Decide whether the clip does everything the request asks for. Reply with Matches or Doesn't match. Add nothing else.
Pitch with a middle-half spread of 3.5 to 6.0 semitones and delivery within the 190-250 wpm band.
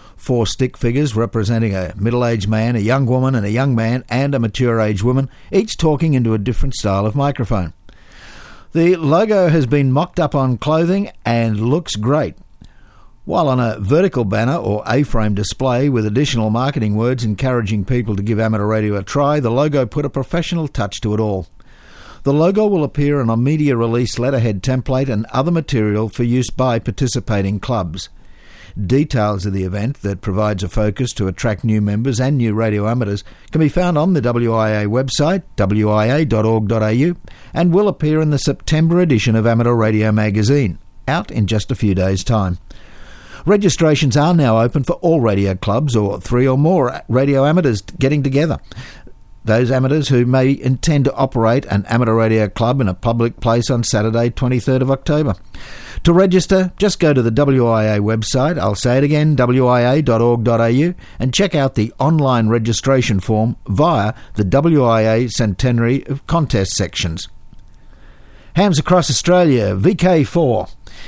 Doesn't match